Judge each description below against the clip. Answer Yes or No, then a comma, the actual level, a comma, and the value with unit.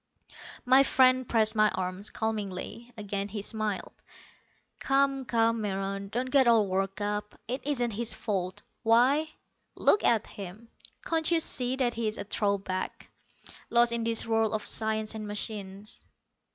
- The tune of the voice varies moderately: Yes, average, 3.0 semitones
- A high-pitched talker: Yes, high, 220 Hz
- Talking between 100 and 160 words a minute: Yes, average, 150 wpm